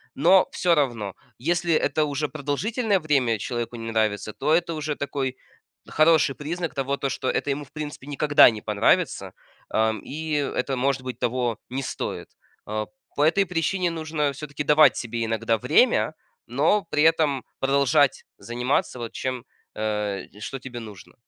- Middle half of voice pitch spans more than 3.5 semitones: Yes, average, 4.4 semitones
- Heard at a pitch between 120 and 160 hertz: Yes, medium, 140 Hz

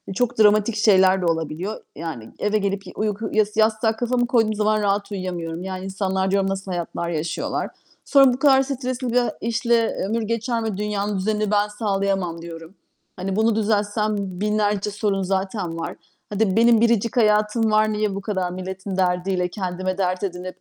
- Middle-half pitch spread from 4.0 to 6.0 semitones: No, narrow, 2.5 semitones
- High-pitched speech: Yes, high, 205 Hz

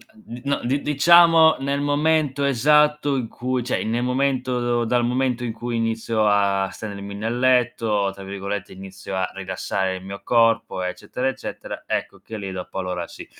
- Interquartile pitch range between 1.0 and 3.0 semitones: No, average, 5.2 semitones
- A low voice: Yes, low, 120 Hz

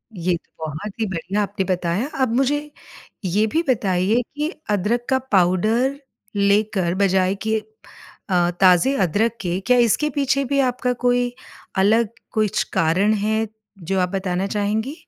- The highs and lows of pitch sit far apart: No, average, 4.6 semitones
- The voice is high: Yes, high, 205 Hz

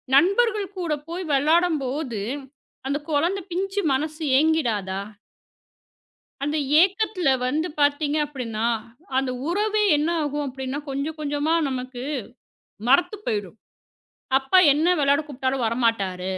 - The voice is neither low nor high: No, very high, 290 Hz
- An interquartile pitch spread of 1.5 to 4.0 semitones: No, average, 4.5 semitones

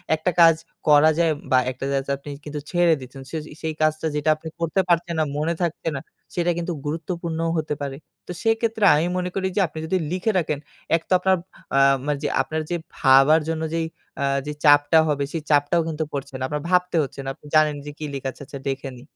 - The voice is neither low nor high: Yes, medium, 155 Hz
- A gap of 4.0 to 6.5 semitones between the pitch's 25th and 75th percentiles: No, average, 2.7 semitones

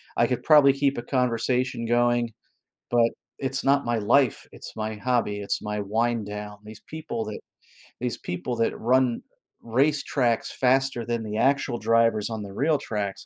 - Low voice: Yes, low, 120 Hz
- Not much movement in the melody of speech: No, average, 3.2 semitones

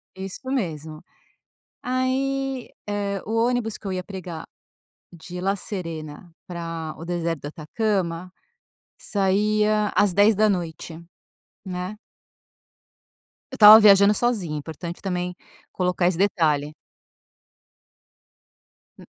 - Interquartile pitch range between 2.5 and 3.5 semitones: No, average, 4.0 semitones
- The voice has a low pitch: No, medium, 185 Hz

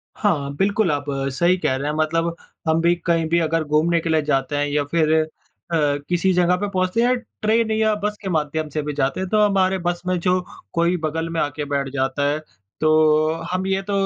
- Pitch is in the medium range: Yes, medium, 165 Hz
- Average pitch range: Yes, average, 3.4 semitones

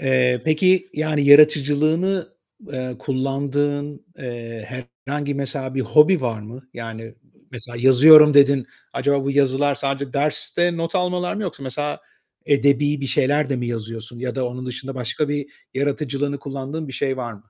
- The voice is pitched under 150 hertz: Yes, medium, 140 Hz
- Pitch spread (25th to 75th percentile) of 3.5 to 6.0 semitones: No, narrow, 2.5 semitones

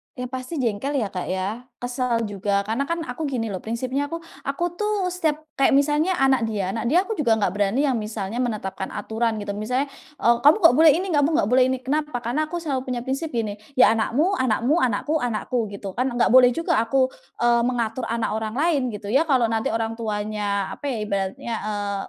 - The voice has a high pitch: Yes, high, 245 Hz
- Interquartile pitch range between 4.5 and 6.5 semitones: Yes, average, 4.8 semitones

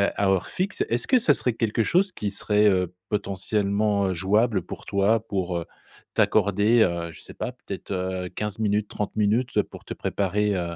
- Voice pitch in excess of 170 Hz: No, low, 105 Hz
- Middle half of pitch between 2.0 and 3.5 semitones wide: Yes, narrow, 2.6 semitones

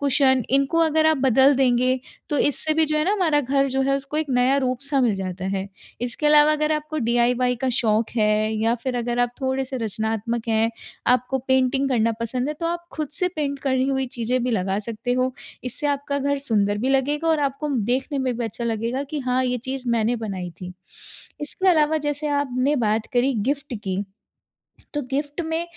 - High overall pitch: Yes, very high, 260 Hz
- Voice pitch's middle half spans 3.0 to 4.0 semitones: Yes, average, 3.6 semitones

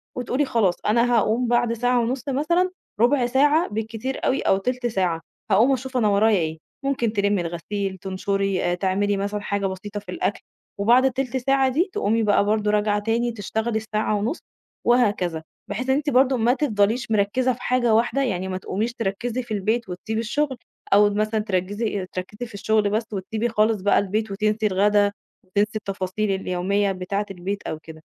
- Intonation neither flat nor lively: Yes, average, 3.5 semitones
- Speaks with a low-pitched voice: No, high, 215 Hz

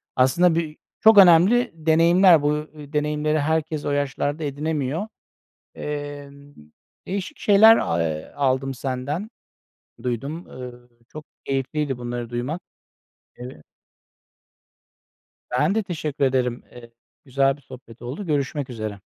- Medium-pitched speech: Yes, medium, 145 Hz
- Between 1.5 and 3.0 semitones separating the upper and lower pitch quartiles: No, average, 3.9 semitones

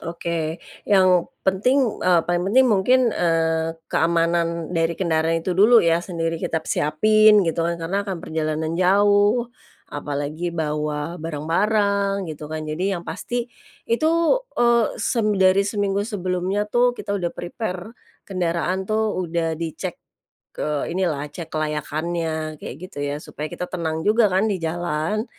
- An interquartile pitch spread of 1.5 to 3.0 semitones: No, average, 3.9 semitones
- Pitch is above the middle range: No, medium, 175 Hz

